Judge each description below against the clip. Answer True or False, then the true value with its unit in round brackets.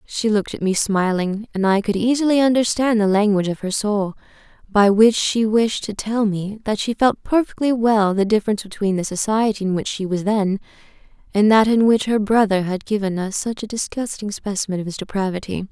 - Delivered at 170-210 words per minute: True (200 wpm)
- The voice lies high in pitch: True (210 Hz)